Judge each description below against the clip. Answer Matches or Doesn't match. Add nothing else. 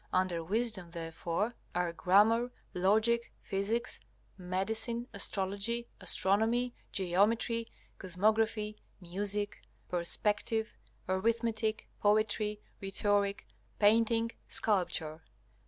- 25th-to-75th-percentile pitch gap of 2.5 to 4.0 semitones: Matches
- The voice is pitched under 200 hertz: Doesn't match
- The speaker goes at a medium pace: Doesn't match